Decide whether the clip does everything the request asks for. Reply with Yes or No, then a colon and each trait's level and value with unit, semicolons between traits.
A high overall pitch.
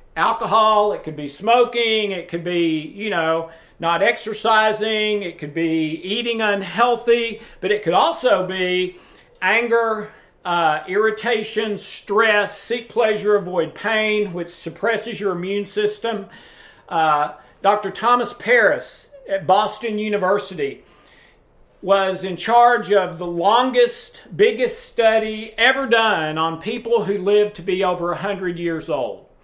Yes: high, 210 Hz